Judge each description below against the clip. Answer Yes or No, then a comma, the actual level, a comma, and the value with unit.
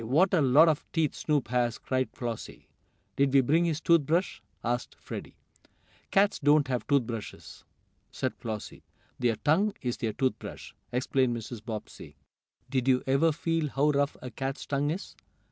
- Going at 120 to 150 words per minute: No, average, 165 wpm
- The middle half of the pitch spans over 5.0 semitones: No, average, 4.0 semitones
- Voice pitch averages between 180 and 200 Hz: No, low, 135 Hz